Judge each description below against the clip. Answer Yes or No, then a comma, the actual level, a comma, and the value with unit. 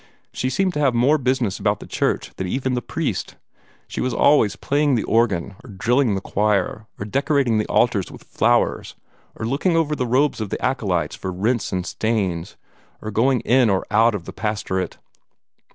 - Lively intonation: No, average, 4.7 semitones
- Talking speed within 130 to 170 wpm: No, average, 185 wpm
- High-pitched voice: No, low, 115 Hz